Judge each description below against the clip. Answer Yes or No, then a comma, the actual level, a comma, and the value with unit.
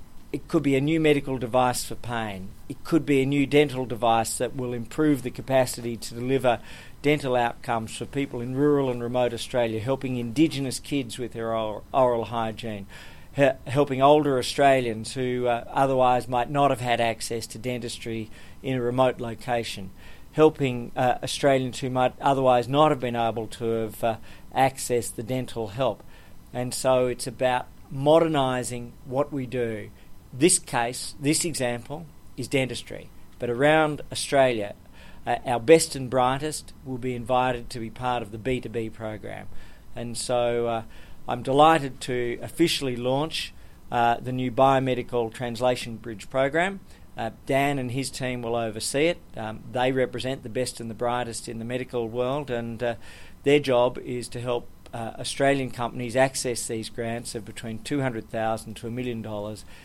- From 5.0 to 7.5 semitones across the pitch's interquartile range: No, narrow, 2.5 semitones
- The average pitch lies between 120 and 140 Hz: Yes, low, 125 Hz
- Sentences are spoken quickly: No, average, 165 wpm